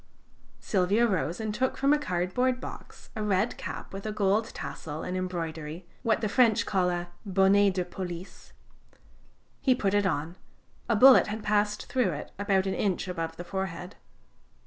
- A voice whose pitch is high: Yes, high, 195 Hz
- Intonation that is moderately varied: Yes, average, 3.2 semitones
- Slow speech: No, average, 170 wpm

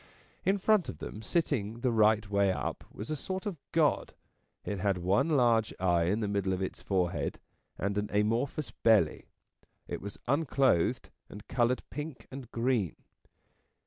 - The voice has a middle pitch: No, low, 110 Hz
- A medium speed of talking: Yes, average, 160 wpm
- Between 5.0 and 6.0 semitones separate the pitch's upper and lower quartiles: Yes, wide, 5.4 semitones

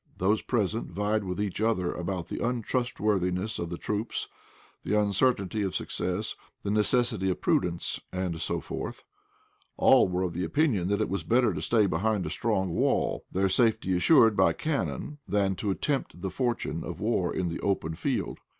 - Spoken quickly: No, average, 170 wpm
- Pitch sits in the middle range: No, low, 100 Hz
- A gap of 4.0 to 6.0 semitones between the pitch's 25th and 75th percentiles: No, average, 3.4 semitones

